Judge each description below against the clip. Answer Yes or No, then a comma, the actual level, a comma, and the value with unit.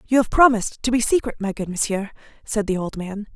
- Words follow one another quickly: Yes, fast, 235 wpm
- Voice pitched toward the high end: Yes, high, 215 Hz